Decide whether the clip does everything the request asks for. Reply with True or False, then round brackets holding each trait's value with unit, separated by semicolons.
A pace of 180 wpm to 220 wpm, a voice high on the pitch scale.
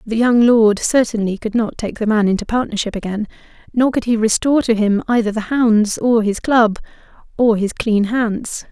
True (185 wpm; 220 Hz)